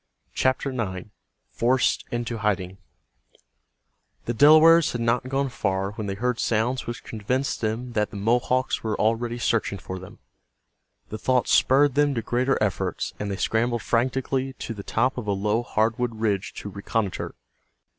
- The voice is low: Yes, low, 115 Hz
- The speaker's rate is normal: Yes, average, 155 wpm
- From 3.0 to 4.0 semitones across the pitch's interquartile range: Yes, average, 3.4 semitones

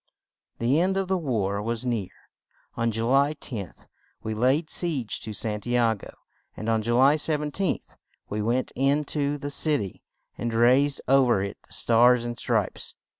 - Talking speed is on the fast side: No, average, 180 wpm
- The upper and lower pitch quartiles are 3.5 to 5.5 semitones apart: Yes, average, 4.2 semitones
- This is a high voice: No, low, 125 Hz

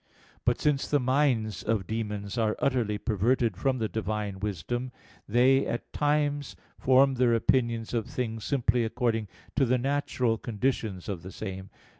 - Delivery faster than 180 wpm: No, average, 150 wpm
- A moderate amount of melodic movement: Yes, average, 3.5 semitones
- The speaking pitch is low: Yes, low, 115 Hz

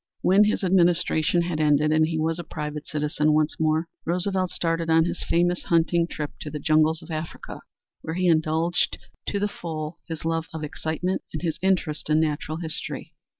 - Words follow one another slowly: No, average, 185 wpm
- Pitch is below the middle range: No, medium, 160 Hz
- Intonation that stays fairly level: Yes, narrow, 2.0 semitones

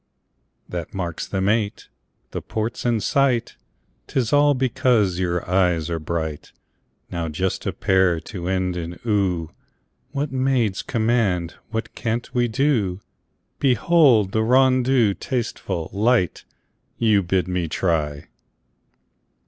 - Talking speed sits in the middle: No, slow, 120 wpm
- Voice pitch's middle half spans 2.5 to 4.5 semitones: No, wide, 5.6 semitones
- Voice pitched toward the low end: Yes, low, 100 Hz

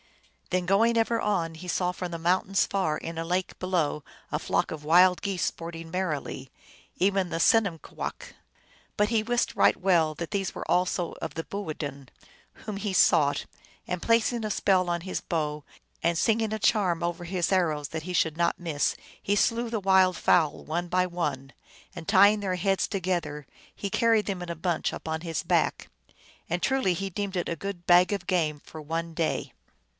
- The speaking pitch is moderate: Yes, medium, 180 Hz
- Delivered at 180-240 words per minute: Yes, average, 190 wpm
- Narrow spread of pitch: No, average, 3.1 semitones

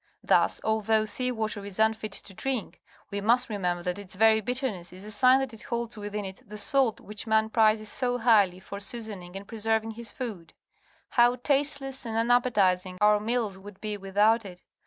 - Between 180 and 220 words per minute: Yes, average, 185 wpm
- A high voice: Yes, high, 220 Hz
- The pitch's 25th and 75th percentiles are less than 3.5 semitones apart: Yes, average, 2.8 semitones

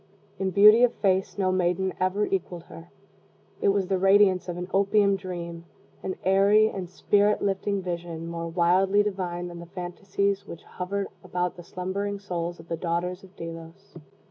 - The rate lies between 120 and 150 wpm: No, average, 170 wpm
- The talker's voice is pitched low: No, medium, 185 Hz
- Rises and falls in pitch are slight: Yes, narrow, 2.2 semitones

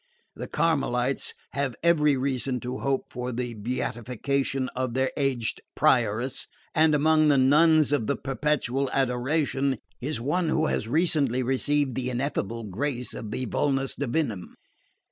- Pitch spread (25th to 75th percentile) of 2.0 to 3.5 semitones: Yes, average, 2.9 semitones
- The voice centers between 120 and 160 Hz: Yes, low, 135 Hz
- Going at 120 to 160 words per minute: Yes, average, 140 wpm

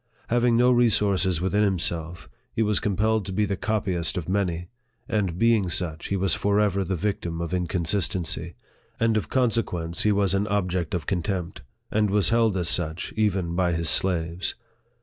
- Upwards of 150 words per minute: Yes, average, 170 wpm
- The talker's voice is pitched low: Yes, very low, 95 Hz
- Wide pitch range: No, average, 3.4 semitones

